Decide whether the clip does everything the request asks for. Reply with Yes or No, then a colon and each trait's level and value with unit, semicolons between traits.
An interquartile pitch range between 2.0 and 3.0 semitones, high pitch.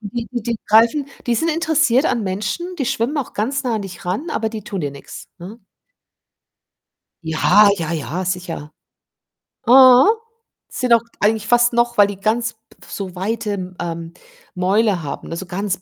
No: average, 4.7 semitones; high, 215 Hz